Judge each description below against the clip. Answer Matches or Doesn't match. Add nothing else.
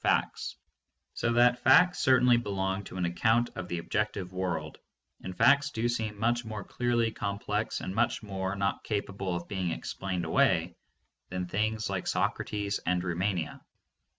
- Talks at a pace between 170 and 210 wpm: Doesn't match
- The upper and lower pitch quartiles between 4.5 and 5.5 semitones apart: Doesn't match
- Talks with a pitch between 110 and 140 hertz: Doesn't match